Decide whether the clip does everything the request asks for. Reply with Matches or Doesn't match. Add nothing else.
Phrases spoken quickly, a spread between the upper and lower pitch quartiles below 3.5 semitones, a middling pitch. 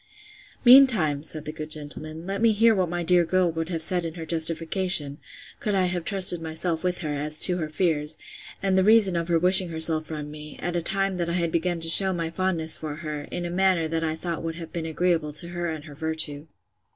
Matches